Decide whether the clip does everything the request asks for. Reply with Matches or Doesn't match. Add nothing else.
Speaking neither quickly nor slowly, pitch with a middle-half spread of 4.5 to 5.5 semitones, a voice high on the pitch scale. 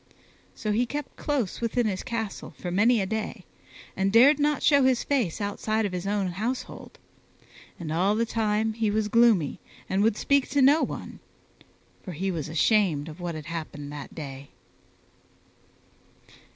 Matches